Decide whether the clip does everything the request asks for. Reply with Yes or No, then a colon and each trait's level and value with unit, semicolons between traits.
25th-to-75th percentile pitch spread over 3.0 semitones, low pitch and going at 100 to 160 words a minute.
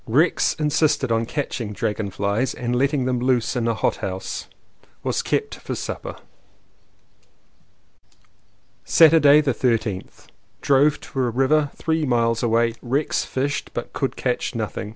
Yes: average, 3.8 semitones; low, 125 Hz; slow, 135 wpm